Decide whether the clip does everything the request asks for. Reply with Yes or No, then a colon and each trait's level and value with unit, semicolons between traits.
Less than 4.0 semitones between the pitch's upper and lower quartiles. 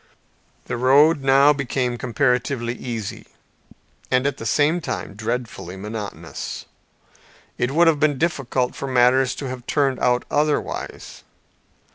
Yes: average, 2.8 semitones